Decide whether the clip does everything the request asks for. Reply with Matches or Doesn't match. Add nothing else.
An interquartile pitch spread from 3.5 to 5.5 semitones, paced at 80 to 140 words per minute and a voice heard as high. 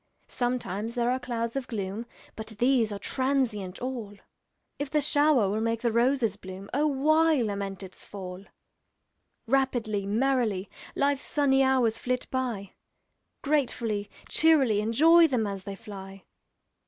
Matches